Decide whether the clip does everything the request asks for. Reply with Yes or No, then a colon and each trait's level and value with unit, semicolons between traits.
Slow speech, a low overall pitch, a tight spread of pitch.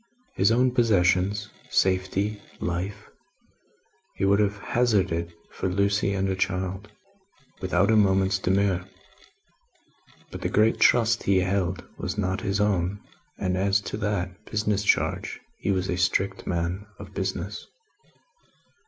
Yes: slow, 130 wpm; very low, 95 Hz; narrow, 1.9 semitones